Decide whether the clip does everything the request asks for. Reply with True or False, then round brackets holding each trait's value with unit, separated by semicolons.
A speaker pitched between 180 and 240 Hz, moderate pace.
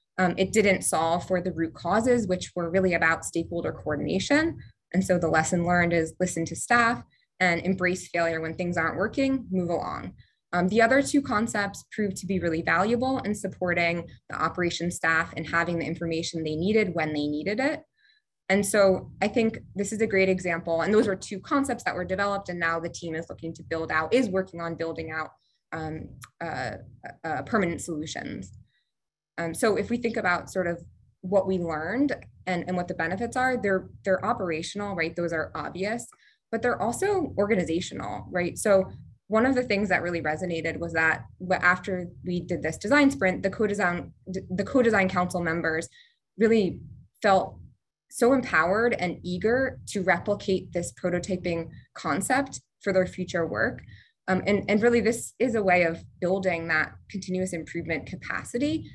True (185 Hz; 175 wpm)